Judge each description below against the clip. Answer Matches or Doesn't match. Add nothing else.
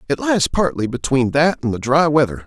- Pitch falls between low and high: Matches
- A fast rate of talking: Matches